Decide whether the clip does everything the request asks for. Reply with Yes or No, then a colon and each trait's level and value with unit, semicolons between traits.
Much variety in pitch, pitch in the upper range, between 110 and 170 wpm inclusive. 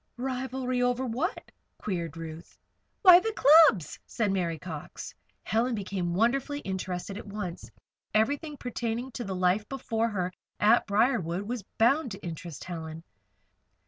Yes: wide, 5.7 semitones; high, 215 Hz; slow, 135 wpm